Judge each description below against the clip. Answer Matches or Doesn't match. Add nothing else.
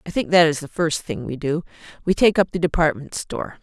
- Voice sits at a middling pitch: Matches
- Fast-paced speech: Matches